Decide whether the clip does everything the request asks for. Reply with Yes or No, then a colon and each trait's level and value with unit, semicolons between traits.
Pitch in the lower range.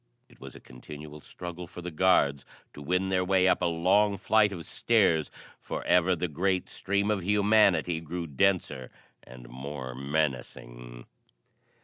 Yes: very low, 85 Hz